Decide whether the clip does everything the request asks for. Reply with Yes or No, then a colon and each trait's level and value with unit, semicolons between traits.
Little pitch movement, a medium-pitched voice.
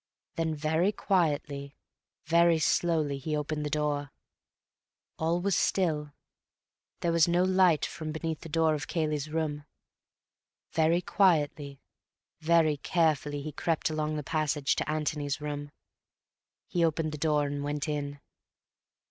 Yes: narrow, 2.0 semitones; medium, 155 Hz